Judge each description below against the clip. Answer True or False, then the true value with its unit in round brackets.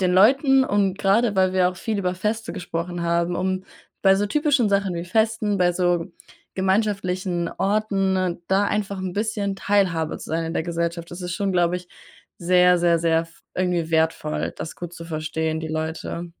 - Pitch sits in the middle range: True (180 Hz)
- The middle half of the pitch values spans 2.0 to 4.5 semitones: True (2.8 semitones)